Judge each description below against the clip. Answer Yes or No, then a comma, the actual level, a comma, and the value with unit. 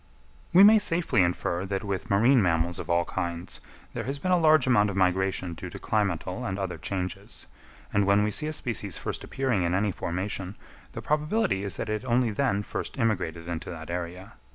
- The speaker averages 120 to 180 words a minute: No, average, 200 wpm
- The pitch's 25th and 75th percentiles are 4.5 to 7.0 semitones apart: Yes, wide, 5.6 semitones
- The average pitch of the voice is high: No, low, 100 Hz